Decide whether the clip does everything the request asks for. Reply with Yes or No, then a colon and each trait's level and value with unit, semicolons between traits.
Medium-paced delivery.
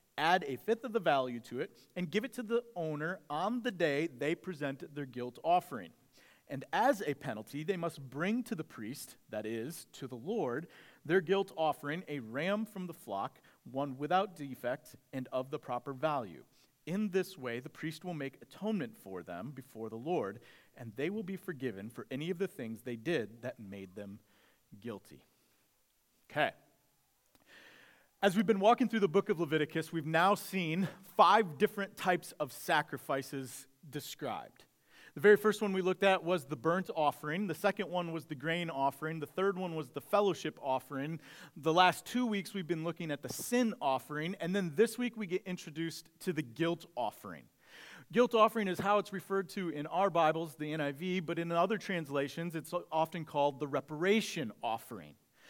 Yes: average, 185 wpm